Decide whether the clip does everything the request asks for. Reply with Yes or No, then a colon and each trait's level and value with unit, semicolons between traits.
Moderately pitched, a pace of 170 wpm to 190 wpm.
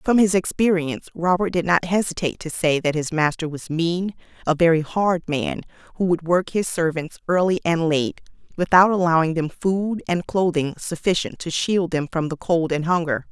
Yes: medium, 170 Hz; average, 185 wpm